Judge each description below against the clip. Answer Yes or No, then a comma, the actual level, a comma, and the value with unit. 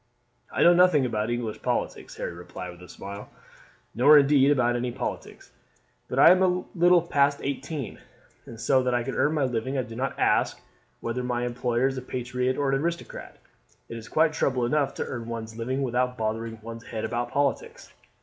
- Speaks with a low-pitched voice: Yes, low, 125 Hz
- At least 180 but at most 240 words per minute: Yes, average, 190 wpm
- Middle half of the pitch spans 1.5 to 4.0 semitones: Yes, average, 3.4 semitones